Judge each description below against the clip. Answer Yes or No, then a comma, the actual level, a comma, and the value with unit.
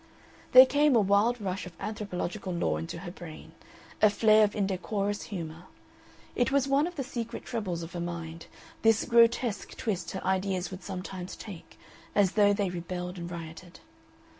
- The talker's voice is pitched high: Yes, high, 195 Hz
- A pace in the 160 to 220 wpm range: Yes, average, 165 wpm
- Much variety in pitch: No, average, 3.8 semitones